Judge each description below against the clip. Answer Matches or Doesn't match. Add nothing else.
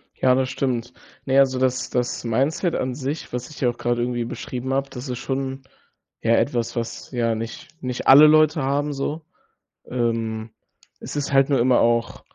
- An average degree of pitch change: Doesn't match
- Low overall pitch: Matches